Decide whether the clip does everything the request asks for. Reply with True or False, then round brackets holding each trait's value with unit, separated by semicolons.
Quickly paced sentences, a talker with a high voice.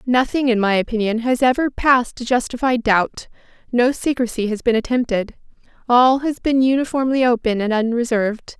False (155 wpm; 240 Hz)